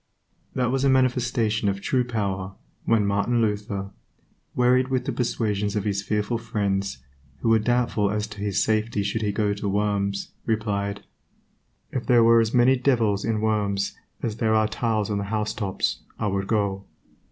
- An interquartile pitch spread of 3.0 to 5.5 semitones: No, narrow, 2.5 semitones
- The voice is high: No, low, 105 Hz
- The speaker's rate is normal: Yes, average, 170 wpm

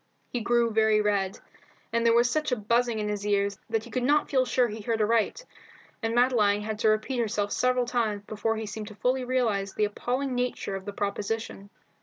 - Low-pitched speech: No, high, 225 Hz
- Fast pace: Yes, fast, 210 wpm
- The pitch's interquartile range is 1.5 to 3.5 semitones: Yes, average, 2.9 semitones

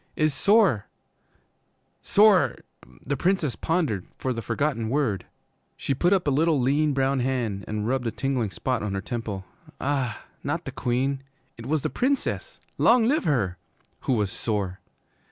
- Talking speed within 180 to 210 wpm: No, average, 160 wpm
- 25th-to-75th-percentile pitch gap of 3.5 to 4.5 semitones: No, wide, 5.6 semitones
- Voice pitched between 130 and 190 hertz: Yes, low, 135 Hz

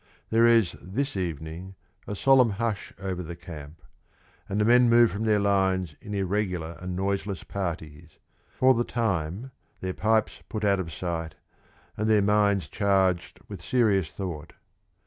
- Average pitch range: Yes, average, 3.7 semitones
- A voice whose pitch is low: Yes, very low, 95 Hz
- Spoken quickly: No, average, 150 wpm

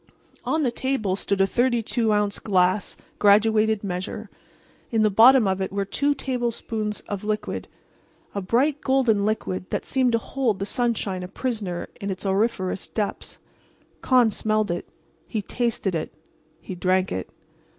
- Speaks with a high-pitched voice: Yes, high, 215 Hz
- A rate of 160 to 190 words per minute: No, average, 150 wpm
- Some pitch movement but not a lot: Yes, average, 3.6 semitones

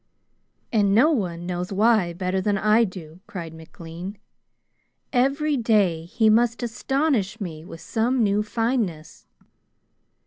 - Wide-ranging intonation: No, average, 5.0 semitones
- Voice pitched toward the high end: Yes, high, 205 Hz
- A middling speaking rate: No, slow, 125 wpm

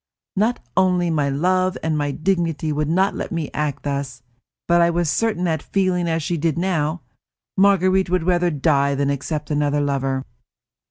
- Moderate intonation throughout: Yes, average, 3.8 semitones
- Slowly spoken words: No, average, 170 wpm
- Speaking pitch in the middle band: Yes, medium, 165 Hz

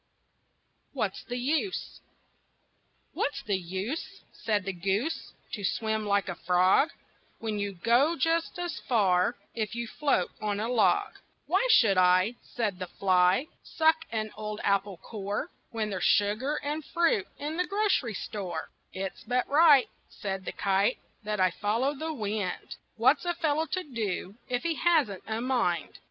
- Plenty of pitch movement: Yes, wide, 6.8 semitones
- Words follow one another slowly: No, average, 155 wpm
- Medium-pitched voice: No, high, 220 Hz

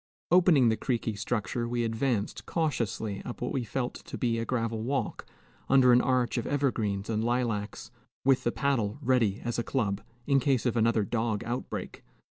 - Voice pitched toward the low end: Yes, low, 120 Hz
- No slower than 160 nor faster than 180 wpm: Yes, average, 175 wpm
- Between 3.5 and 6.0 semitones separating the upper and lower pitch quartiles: No, average, 2.7 semitones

